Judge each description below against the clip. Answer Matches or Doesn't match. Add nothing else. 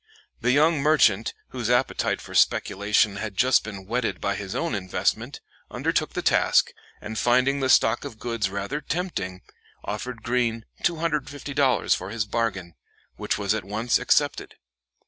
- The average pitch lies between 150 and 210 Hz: Doesn't match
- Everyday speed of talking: Matches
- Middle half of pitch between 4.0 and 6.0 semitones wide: Matches